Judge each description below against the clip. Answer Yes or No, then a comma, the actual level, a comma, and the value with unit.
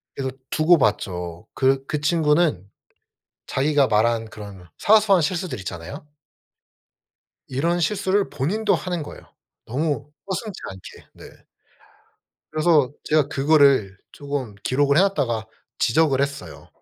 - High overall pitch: No, medium, 145 Hz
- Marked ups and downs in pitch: Yes, wide, 6.2 semitones